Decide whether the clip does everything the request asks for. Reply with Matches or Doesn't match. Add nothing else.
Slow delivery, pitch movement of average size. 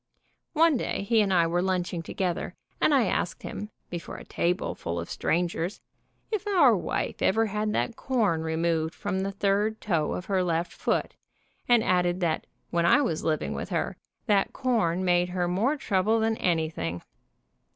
Doesn't match